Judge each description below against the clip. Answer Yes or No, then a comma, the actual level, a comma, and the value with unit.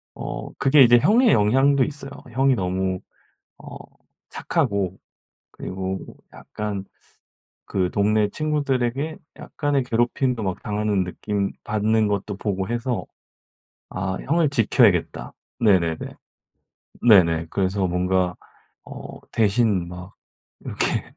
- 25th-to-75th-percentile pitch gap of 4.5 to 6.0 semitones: Yes, average, 5.2 semitones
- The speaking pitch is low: Yes, low, 105 Hz